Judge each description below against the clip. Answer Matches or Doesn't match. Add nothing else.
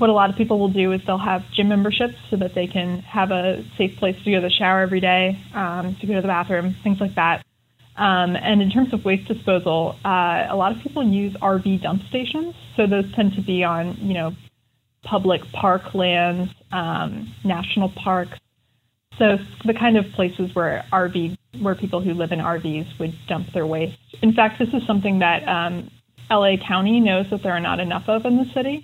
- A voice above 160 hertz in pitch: Matches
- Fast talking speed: Matches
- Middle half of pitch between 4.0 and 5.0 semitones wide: Doesn't match